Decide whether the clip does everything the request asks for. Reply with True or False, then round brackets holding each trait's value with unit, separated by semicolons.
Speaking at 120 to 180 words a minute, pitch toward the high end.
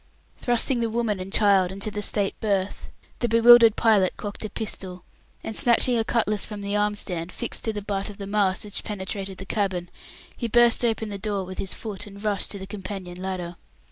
False (205 wpm; 205 Hz)